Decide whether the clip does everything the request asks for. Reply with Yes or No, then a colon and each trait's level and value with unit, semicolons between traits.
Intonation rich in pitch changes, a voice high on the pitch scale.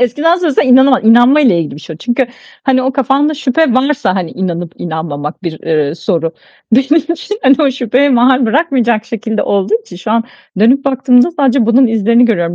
Yes: wide, 5.9 semitones; high, 245 Hz